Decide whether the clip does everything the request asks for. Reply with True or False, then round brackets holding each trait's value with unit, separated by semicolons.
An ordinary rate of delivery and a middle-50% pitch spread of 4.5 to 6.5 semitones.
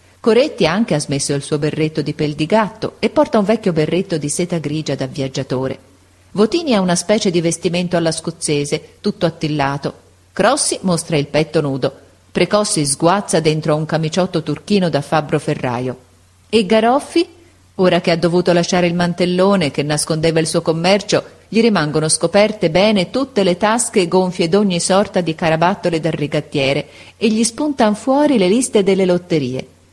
True (160 wpm; 4.8 semitones)